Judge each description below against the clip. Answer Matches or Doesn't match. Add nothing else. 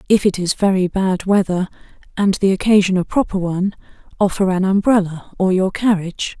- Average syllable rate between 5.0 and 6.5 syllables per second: Matches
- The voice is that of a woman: Matches